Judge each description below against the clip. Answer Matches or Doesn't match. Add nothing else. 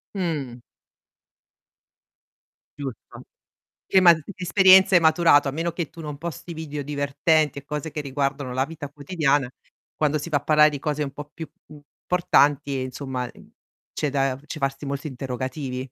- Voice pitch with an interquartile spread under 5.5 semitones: Matches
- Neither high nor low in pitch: Matches